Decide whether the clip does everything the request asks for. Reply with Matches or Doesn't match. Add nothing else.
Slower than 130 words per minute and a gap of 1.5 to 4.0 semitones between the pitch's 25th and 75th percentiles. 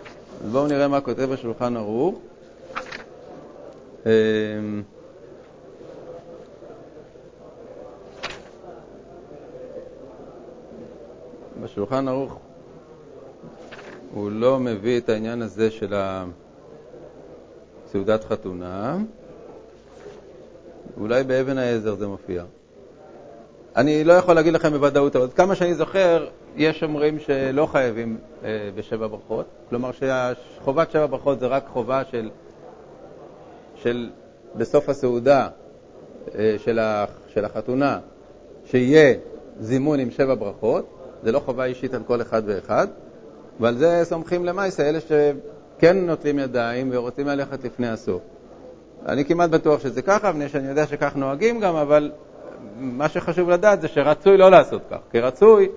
Doesn't match